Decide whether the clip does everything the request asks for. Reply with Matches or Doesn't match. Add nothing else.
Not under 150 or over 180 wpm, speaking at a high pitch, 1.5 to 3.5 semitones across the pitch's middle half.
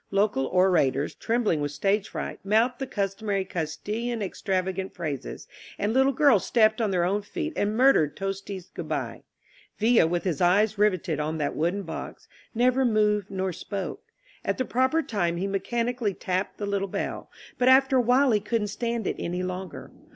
Doesn't match